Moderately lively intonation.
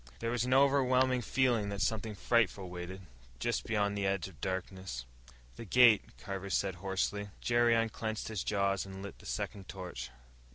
Yes: average, 3.3 semitones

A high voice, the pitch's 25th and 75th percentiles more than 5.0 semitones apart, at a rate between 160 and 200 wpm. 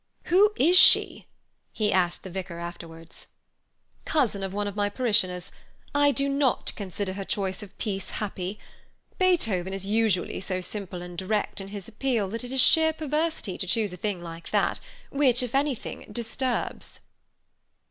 Yes: high, 205 Hz; wide, 5.6 semitones; average, 165 wpm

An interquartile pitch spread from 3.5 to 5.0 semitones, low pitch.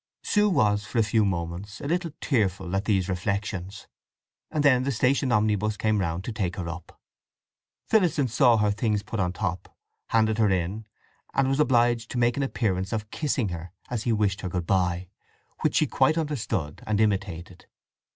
Yes: average, 4.3 semitones; low, 105 Hz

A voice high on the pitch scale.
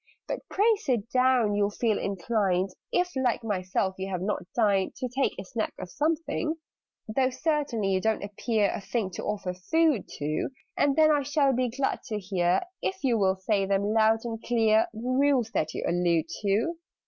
Yes: high, 220 Hz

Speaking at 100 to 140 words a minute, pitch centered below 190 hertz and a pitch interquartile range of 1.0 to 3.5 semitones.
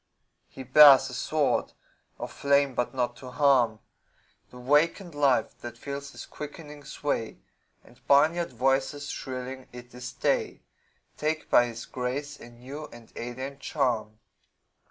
Yes: slow, 135 wpm; low, 135 Hz; average, 2.8 semitones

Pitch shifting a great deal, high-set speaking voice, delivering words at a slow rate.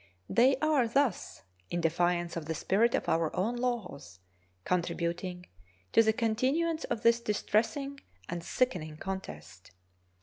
Yes: wide, 6.0 semitones; high, 210 Hz; slow, 130 wpm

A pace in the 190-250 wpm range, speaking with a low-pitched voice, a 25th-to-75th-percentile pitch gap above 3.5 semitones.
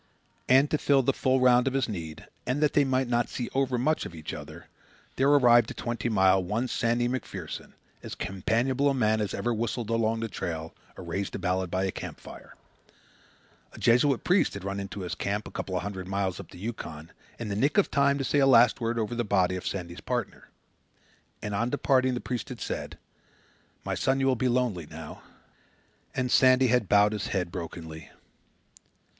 Yes: average, 200 wpm; low, 115 Hz; average, 5.0 semitones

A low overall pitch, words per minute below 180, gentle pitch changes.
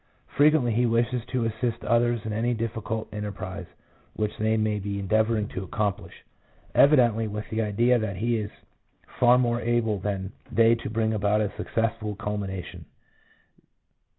Yes: low, 110 Hz; average, 150 wpm; narrow, 2.2 semitones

